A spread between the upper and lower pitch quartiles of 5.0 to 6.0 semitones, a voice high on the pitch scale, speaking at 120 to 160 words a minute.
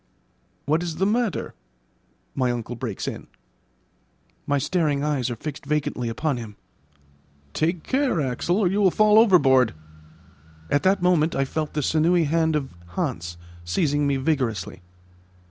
No: average, 5.3 semitones; medium, 150 Hz; average, 145 wpm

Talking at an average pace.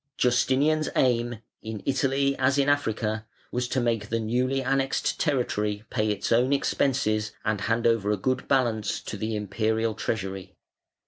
Yes: average, 150 wpm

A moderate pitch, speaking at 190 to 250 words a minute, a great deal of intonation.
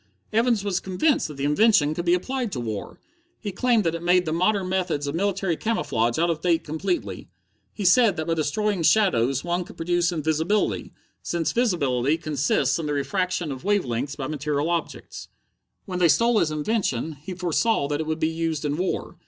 No: medium, 170 Hz; average, 195 wpm; average, 4.6 semitones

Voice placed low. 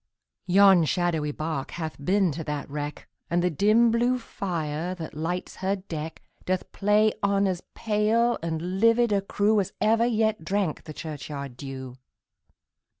No: medium, 180 Hz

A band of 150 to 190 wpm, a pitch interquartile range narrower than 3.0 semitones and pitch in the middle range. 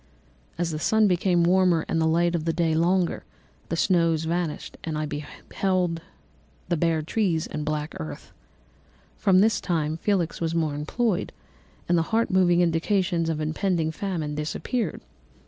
Yes: average, 155 wpm; narrow, 2.6 semitones; medium, 170 Hz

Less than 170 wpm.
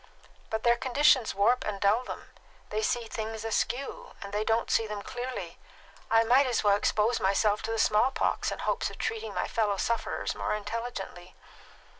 No: average, 180 wpm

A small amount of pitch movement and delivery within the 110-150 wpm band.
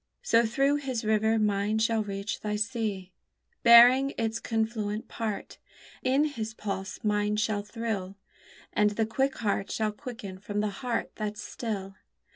Yes: narrow, 2.0 semitones; average, 145 wpm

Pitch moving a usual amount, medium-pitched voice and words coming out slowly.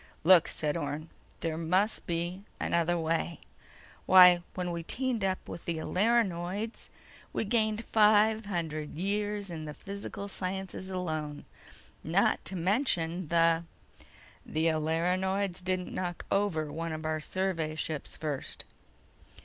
Yes: average, 3.4 semitones; medium, 175 Hz; slow, 125 wpm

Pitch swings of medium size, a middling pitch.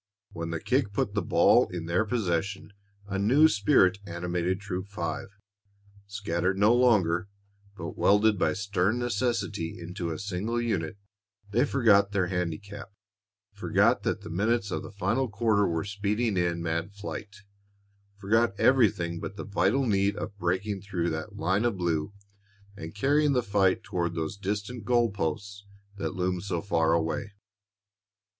No: average, 3.3 semitones; low, 100 Hz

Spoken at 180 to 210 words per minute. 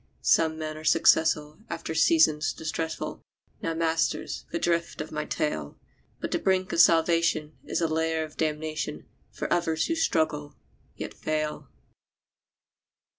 No: slow, 135 wpm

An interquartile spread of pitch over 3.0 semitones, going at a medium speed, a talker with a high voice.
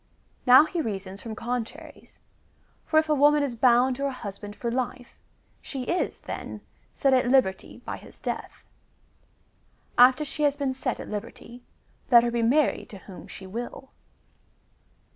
Yes: average, 3.4 semitones; average, 160 wpm; very high, 250 Hz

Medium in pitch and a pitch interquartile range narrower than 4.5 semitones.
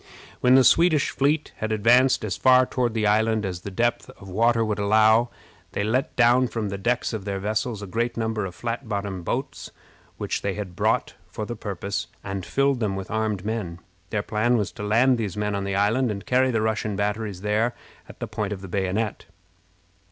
No: low, 110 Hz; average, 2.9 semitones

